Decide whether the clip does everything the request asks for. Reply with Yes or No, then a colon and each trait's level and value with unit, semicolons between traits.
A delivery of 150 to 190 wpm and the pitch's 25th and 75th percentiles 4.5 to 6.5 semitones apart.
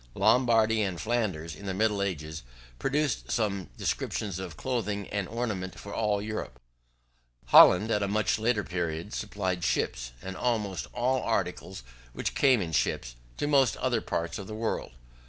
No: average, 155 wpm; average, 3.8 semitones